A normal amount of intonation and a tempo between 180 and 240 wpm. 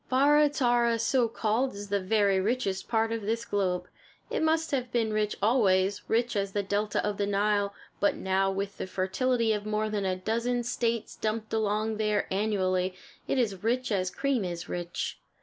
Yes: average, 3.0 semitones; average, 185 wpm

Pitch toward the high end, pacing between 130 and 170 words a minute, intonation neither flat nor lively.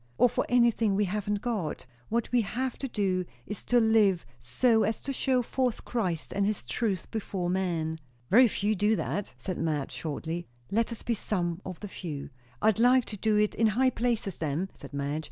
No: high, 210 Hz; average, 195 wpm; average, 4.6 semitones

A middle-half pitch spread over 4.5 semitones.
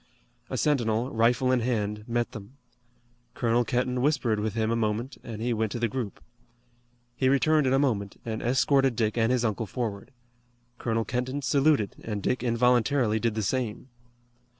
No: average, 2.7 semitones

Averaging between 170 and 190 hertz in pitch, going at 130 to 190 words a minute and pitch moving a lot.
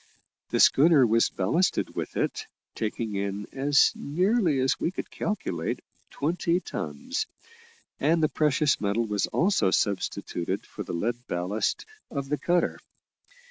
No: low, 135 Hz; slow, 135 wpm; wide, 8.0 semitones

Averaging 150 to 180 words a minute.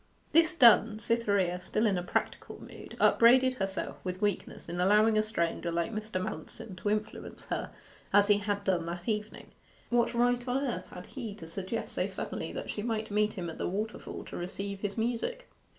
No: average, 190 wpm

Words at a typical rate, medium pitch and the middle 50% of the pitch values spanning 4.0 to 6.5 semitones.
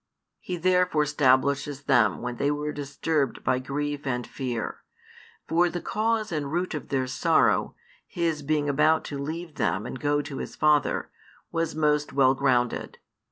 No: average, 160 wpm; medium, 145 Hz; average, 2.9 semitones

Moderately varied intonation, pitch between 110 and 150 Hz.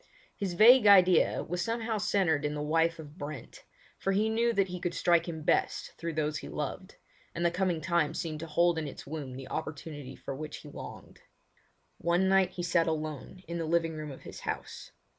No: average, 3.3 semitones; medium, 170 Hz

